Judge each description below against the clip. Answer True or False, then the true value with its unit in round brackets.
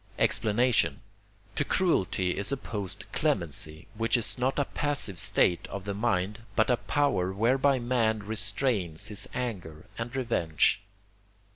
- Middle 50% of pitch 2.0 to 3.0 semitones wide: False (4.9 semitones)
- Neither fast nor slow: False (130 wpm)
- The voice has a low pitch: True (110 Hz)